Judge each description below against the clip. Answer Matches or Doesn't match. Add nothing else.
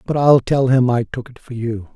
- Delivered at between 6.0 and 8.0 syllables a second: Doesn't match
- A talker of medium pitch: Doesn't match